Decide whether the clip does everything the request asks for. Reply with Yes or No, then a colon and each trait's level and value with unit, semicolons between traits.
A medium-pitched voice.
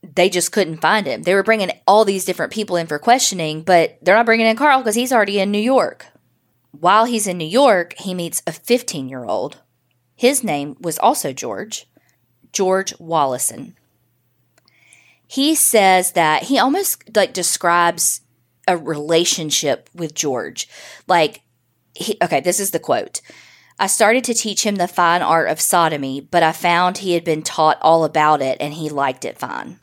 Yes: medium, 175 Hz